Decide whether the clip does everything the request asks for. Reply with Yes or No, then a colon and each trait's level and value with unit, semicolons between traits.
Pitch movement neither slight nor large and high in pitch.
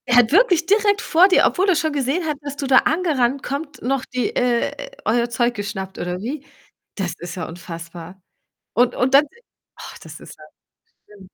No: wide, 7.3 semitones; very high, 255 Hz